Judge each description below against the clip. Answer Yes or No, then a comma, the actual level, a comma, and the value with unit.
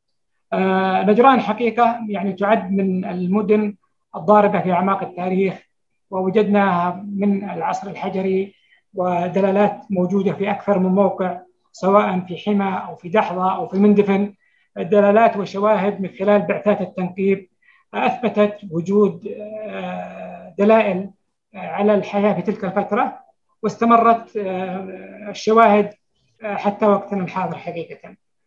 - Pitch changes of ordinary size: No, narrow, 1.8 semitones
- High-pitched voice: Yes, high, 200 Hz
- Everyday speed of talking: Yes, average, 105 wpm